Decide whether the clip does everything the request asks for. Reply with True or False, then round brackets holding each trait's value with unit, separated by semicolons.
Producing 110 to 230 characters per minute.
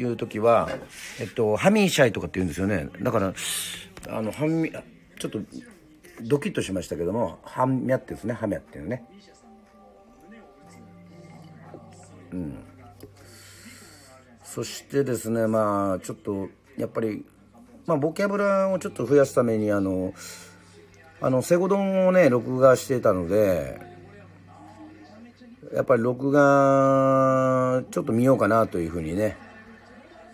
False (270 characters per minute)